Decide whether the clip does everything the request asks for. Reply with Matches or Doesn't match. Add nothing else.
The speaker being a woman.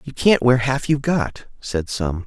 Doesn't match